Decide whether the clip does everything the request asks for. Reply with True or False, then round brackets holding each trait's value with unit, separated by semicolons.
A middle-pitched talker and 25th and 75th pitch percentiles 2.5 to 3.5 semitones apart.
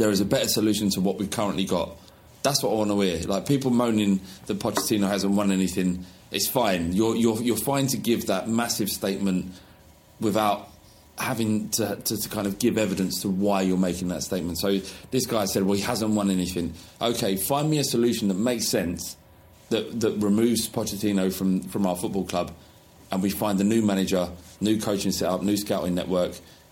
False (100 Hz; 2.9 semitones)